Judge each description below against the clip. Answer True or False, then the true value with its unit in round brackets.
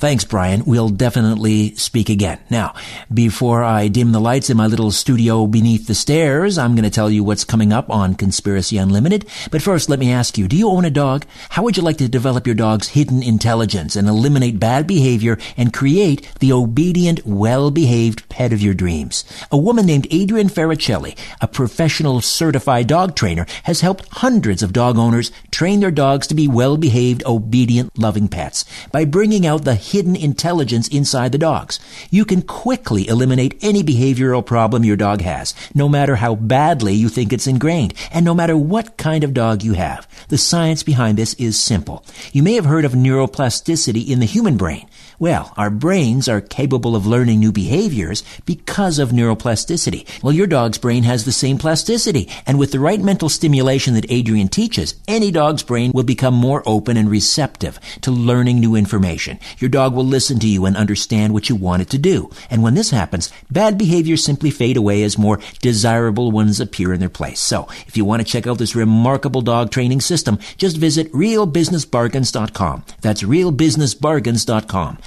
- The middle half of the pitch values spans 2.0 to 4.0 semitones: False (5.6 semitones)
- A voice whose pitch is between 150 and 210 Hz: False (125 Hz)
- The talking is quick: False (185 wpm)